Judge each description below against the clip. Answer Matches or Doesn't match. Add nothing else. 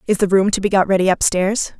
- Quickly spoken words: Matches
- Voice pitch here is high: Matches